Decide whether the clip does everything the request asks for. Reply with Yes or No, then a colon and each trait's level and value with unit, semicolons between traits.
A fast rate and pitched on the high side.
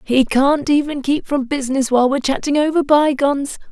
No: average, 180 wpm; very high, 275 Hz